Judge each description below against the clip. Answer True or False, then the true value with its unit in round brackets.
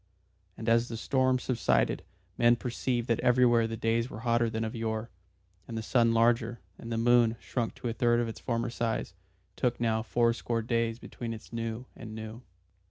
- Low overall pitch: True (115 Hz)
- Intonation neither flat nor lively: False (1.0 semitones)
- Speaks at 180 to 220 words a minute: True (185 wpm)